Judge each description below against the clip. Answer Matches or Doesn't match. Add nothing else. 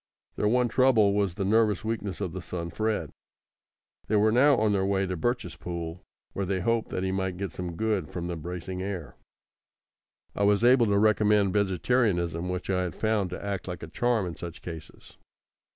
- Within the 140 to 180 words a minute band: Doesn't match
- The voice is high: Doesn't match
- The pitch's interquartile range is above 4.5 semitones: Doesn't match